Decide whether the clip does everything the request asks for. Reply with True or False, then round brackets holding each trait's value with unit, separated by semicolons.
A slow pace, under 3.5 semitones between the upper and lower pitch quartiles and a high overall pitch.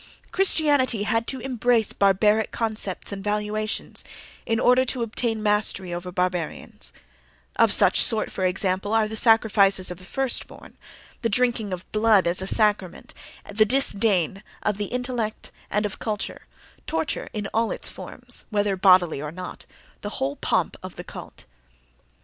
False (155 wpm; 2.9 semitones; 210 Hz)